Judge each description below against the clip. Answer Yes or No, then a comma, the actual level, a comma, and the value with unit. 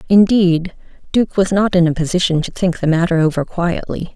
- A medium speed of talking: Yes, average, 190 wpm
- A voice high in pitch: No, medium, 175 Hz